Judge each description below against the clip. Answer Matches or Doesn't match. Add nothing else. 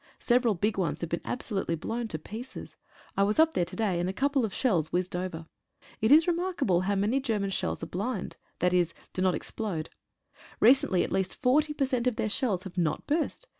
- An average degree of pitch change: Doesn't match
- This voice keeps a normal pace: Doesn't match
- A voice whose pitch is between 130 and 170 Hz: Doesn't match